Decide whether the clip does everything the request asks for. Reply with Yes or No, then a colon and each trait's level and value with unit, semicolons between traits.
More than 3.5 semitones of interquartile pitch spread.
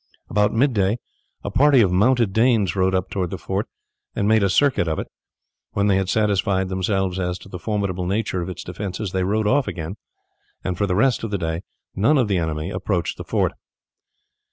No: average, 3.0 semitones